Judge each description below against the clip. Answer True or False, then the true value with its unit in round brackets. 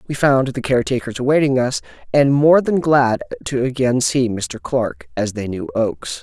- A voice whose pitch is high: False (125 Hz)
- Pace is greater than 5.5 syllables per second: False (4.7 syllables/s)